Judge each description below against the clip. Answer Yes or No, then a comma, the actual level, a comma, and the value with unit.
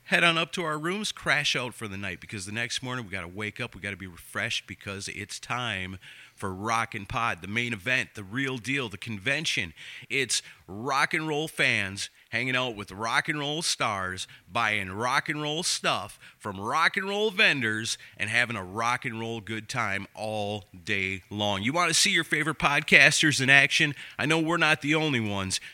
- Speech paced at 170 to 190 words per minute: No, fast, 205 wpm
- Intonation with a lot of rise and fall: Yes, wide, 6.6 semitones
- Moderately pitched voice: No, low, 120 Hz